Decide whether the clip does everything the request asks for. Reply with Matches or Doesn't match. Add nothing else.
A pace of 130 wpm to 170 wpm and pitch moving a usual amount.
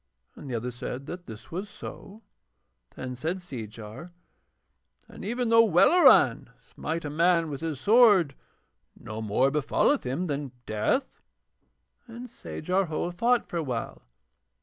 Doesn't match